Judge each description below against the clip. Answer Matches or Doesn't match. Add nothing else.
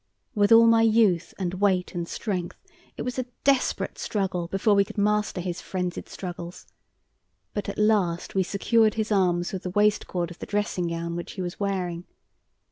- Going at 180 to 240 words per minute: Matches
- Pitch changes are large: Doesn't match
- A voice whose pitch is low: Doesn't match